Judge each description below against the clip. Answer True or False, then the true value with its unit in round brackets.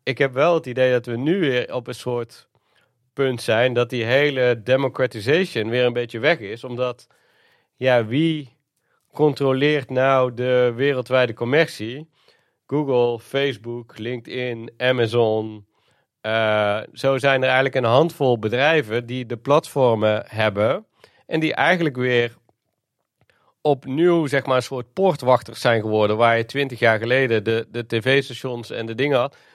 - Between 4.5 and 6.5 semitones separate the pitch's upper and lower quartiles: False (2.6 semitones)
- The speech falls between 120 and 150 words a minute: True (145 wpm)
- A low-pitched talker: True (125 Hz)